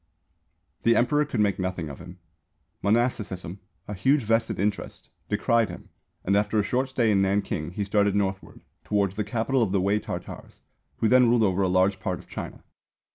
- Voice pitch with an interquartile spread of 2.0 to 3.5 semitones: Yes, average, 3.2 semitones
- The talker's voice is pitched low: Yes, low, 105 Hz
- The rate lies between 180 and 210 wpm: Yes, average, 185 wpm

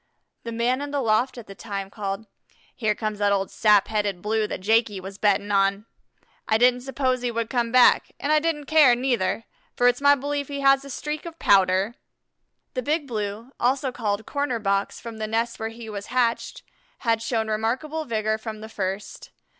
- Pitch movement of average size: Yes, average, 3.6 semitones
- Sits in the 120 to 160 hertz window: No, high, 230 Hz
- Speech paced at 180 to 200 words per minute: Yes, average, 195 wpm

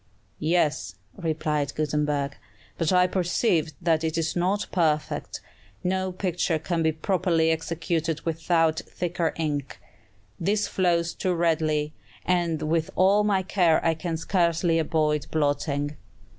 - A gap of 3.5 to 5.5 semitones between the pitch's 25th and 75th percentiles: No, narrow, 2.4 semitones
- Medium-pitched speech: Yes, medium, 165 Hz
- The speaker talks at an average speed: No, slow, 125 wpm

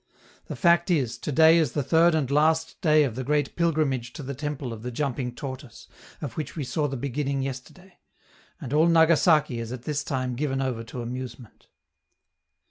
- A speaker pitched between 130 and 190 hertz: Yes, medium, 140 Hz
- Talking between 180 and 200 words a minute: Yes, average, 190 wpm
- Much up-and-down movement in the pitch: No, average, 3.6 semitones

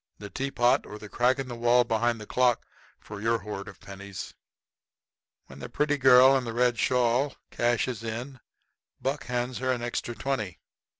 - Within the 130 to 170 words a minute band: No, average, 180 wpm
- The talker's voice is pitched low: Yes, low, 120 Hz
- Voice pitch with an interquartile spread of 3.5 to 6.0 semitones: No, narrow, 2.5 semitones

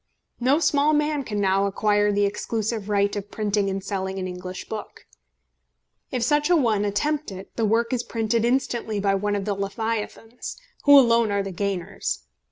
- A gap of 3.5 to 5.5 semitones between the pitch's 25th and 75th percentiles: No, average, 3.1 semitones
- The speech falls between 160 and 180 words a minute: Yes, average, 175 wpm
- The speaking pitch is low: No, high, 210 Hz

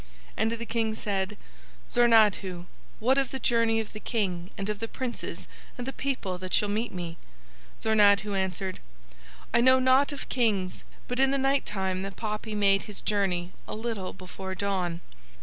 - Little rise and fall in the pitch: No, average, 3.7 semitones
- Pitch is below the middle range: No, high, 210 Hz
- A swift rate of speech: No, average, 170 wpm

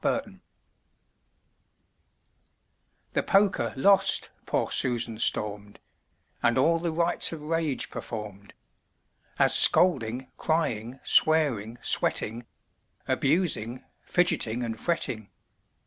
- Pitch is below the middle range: Yes, low, 130 Hz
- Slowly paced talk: Yes, slow, 85 wpm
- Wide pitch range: Yes, wide, 6.6 semitones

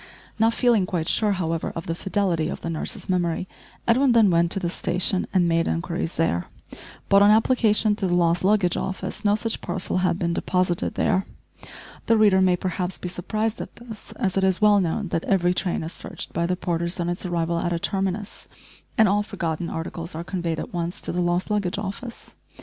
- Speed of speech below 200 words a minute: No, fast, 205 wpm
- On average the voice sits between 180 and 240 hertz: Yes, medium, 185 Hz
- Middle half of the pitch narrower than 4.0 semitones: Yes, average, 3.2 semitones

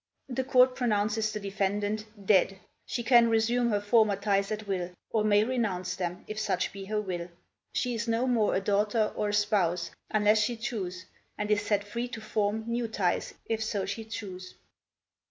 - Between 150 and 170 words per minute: No, average, 185 wpm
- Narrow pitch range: Yes, narrow, 2.3 semitones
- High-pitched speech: Yes, high, 210 Hz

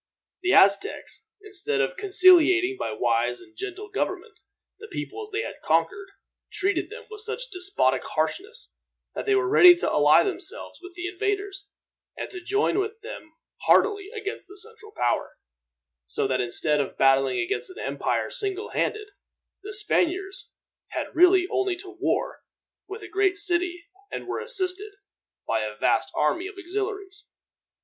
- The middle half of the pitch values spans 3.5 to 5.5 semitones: No, average, 2.8 semitones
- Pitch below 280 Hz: No, very high, 390 Hz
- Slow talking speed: No, average, 155 wpm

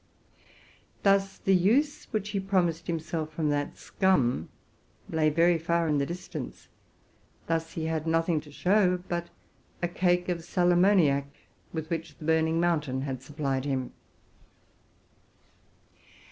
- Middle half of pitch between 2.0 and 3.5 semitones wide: Yes, average, 2.8 semitones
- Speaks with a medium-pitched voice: Yes, medium, 165 Hz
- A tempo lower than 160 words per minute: Yes, average, 145 wpm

